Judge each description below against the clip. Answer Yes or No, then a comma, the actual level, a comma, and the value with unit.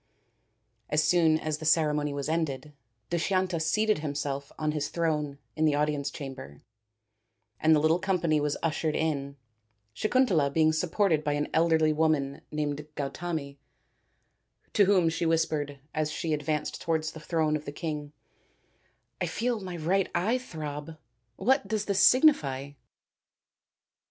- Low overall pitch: No, medium, 155 Hz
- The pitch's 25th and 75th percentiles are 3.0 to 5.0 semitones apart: No, narrow, 2.5 semitones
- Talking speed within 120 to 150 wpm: Yes, average, 145 wpm